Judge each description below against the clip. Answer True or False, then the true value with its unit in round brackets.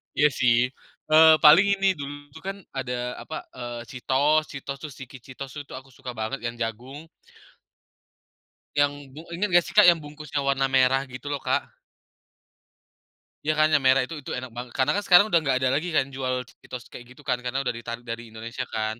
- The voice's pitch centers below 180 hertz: True (135 Hz)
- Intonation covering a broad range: False (3.5 semitones)